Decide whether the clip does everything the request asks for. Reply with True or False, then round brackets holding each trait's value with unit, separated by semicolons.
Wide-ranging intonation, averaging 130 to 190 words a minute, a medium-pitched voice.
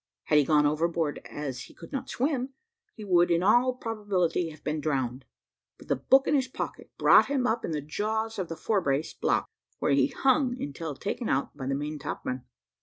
False (8.1 semitones; 205 wpm; 170 Hz)